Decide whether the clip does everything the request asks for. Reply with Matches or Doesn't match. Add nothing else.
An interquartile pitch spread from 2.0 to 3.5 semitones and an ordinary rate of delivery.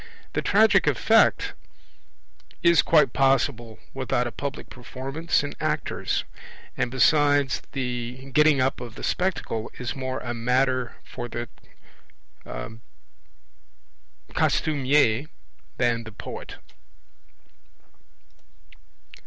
Doesn't match